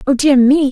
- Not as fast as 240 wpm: No, fast, 250 wpm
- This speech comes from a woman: Yes, female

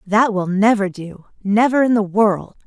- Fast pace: No, average, 180 wpm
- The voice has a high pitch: Yes, high, 210 Hz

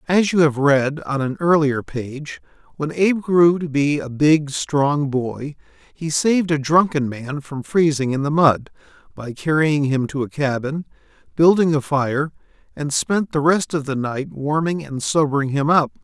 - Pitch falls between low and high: Yes, medium, 150 Hz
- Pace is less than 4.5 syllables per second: Yes, 4.3 syllables/s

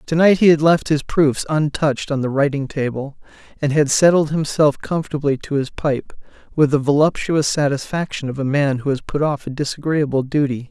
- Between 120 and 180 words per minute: No, average, 190 wpm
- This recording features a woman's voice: No, male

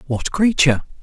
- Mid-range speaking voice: Yes, medium, 155 Hz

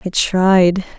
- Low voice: No, medium, 185 Hz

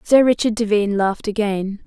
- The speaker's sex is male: No, female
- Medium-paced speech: Yes, average, 160 wpm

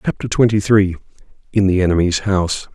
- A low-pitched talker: Yes, very low, 95 Hz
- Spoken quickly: No, slow, 130 wpm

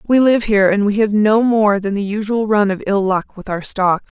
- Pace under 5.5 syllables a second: Yes, 5.2 syllables/s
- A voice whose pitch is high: Yes, high, 205 Hz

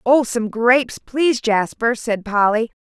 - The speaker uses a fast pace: No, average, 150 wpm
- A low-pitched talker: No, high, 235 Hz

